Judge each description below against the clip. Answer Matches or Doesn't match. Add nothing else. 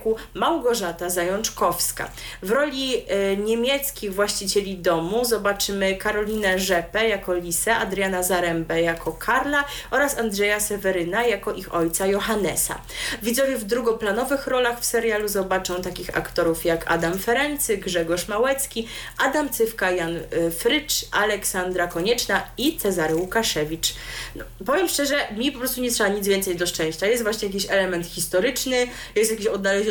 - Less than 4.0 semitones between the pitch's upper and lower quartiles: Doesn't match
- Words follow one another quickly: Doesn't match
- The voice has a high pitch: Matches